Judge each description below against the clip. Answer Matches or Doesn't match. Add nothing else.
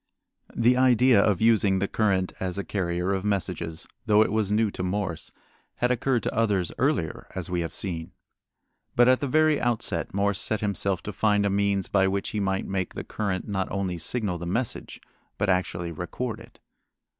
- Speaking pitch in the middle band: Doesn't match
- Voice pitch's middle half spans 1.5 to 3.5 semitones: Matches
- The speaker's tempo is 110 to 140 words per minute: Doesn't match